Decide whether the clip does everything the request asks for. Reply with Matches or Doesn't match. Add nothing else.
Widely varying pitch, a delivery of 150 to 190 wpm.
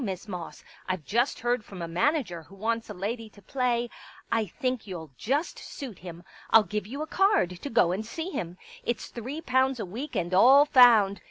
Doesn't match